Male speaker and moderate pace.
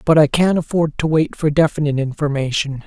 Yes: male; average, 190 wpm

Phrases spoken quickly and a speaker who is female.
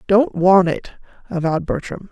No: average, 140 wpm; female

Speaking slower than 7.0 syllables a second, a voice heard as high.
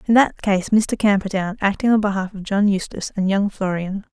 Yes: 5.4 syllables/s; high, 200 Hz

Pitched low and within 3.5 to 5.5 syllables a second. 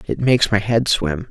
Yes: low, 105 Hz; 5.1 syllables/s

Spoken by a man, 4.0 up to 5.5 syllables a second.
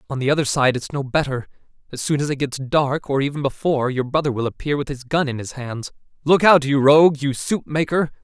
No: male; 5.9 syllables/s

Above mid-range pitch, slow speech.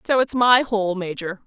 No: high, 210 Hz; fast, 205 wpm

